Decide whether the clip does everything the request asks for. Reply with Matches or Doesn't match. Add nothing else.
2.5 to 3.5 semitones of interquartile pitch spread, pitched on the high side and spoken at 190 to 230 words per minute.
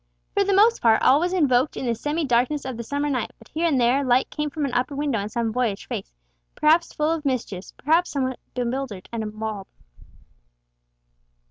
Doesn't match